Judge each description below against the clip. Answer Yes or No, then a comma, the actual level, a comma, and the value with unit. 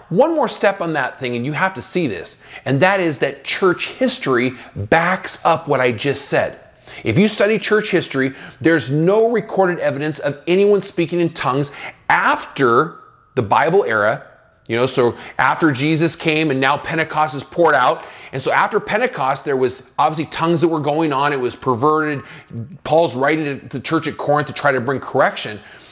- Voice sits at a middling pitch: Yes, medium, 155 Hz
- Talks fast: No, average, 190 wpm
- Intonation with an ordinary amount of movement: Yes, average, 4.1 semitones